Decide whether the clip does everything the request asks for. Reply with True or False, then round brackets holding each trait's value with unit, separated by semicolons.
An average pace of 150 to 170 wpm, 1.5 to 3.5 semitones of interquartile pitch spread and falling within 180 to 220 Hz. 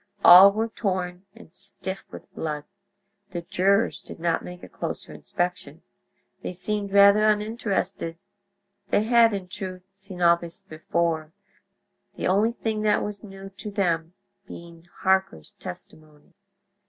False (135 wpm; 3.2 semitones; 190 Hz)